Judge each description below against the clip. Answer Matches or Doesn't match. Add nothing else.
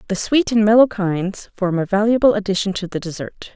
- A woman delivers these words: Matches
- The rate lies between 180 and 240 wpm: Matches